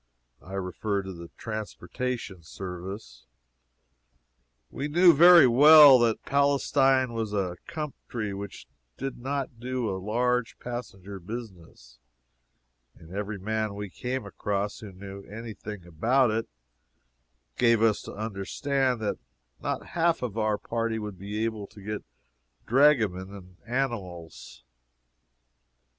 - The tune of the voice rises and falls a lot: No, average, 4.4 semitones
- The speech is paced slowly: Yes, slow, 120 wpm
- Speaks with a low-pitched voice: Yes, low, 110 Hz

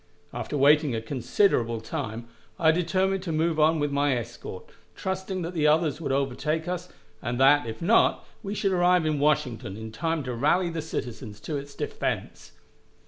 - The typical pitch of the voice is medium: Yes, medium, 150 Hz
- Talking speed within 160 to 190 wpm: Yes, average, 175 wpm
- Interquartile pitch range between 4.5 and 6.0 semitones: Yes, wide, 5.5 semitones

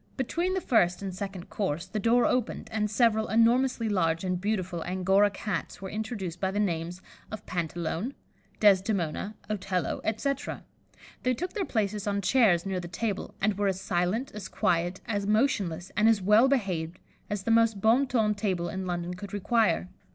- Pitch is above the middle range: Yes, high, 200 Hz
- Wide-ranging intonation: No, average, 3.6 semitones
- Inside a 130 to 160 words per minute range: No, average, 175 wpm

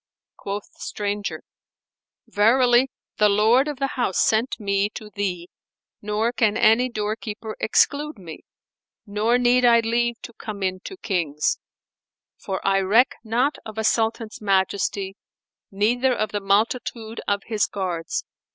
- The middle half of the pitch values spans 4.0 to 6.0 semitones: No, average, 3.0 semitones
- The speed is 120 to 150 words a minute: Yes, average, 140 wpm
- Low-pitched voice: No, high, 215 Hz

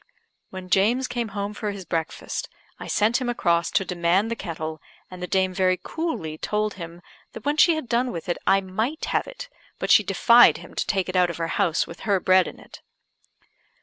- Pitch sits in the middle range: No, high, 195 Hz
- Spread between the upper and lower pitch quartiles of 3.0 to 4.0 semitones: No, average, 4.8 semitones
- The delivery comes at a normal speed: No, fast, 215 wpm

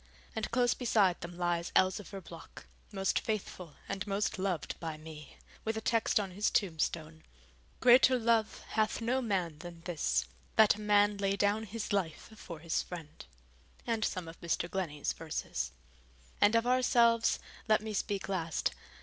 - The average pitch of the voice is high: Yes, high, 195 Hz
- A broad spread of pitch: No, average, 4.4 semitones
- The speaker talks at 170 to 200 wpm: No, average, 160 wpm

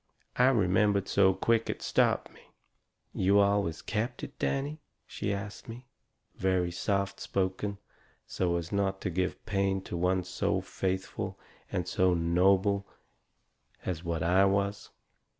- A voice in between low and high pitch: No, very low, 95 Hz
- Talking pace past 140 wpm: No, slow, 135 wpm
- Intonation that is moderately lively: No, narrow, 1.8 semitones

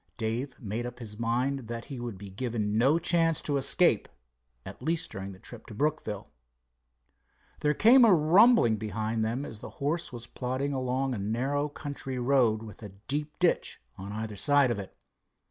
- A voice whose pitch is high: No, low, 125 Hz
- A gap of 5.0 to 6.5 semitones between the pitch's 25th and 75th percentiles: No, average, 4.6 semitones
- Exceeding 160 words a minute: Yes, average, 180 wpm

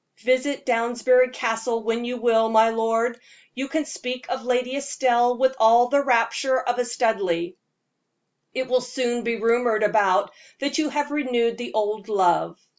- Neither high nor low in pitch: No, high, 240 Hz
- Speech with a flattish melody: Yes, narrow, 2.1 semitones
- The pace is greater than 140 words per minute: Yes, average, 160 wpm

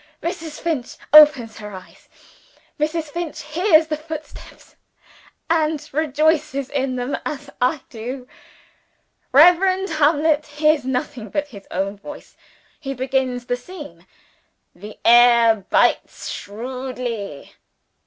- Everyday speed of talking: No, slow, 110 wpm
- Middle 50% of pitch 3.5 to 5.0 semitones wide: Yes, average, 4.0 semitones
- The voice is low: No, very high, 280 Hz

